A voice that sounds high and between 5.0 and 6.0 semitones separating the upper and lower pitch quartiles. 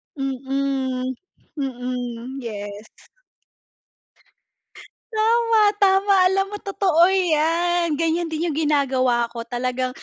Yes: very high, 275 Hz; wide, 5.6 semitones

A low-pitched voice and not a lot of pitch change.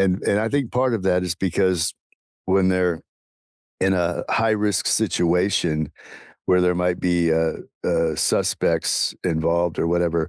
Yes: very low, 90 Hz; narrow, 2.1 semitones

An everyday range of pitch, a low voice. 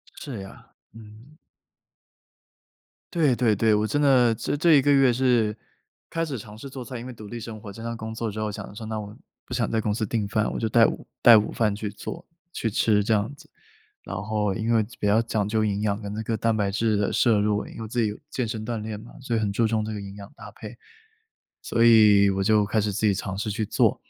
No: narrow, 1.9 semitones; low, 110 Hz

